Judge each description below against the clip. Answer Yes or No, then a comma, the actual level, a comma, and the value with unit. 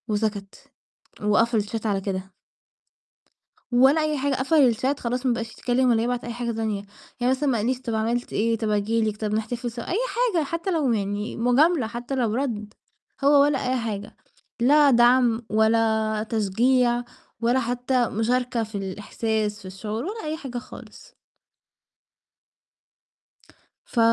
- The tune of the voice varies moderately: Yes, average, 3.0 semitones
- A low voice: No, high, 235 Hz